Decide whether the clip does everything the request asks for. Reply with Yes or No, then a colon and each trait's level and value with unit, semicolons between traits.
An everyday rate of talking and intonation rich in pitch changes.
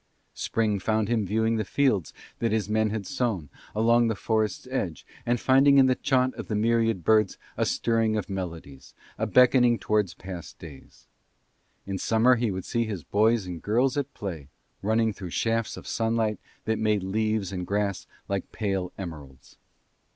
No: average, 170 wpm; average, 3.1 semitones